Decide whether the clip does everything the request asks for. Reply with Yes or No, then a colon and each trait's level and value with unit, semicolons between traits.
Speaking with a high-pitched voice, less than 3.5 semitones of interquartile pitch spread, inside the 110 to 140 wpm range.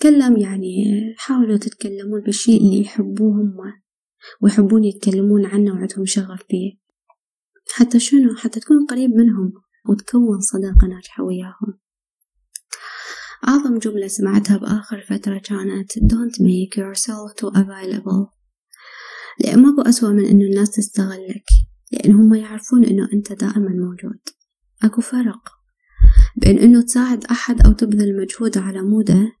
Yes: high, 210 Hz; average, 2.7 semitones; average, 120 wpm